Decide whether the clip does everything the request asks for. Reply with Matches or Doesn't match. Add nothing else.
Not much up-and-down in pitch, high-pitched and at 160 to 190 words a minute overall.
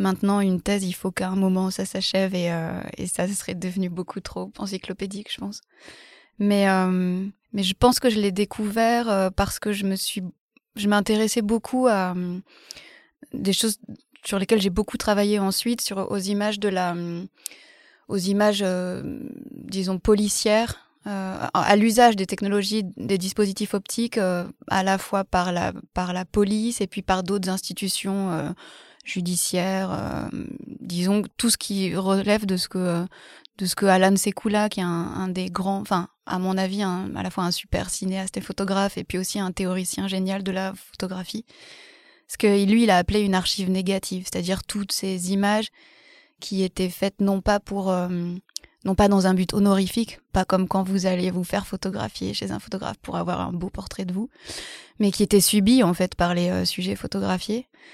Matches